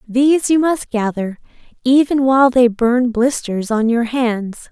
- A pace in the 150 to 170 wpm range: Yes, average, 155 wpm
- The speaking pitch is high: Yes, high, 245 Hz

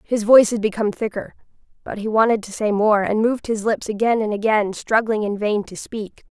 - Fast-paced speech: Yes, fast, 220 wpm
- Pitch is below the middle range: No, high, 215 Hz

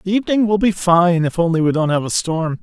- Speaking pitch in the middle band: Yes, medium, 180 Hz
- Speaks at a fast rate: Yes, fast, 275 wpm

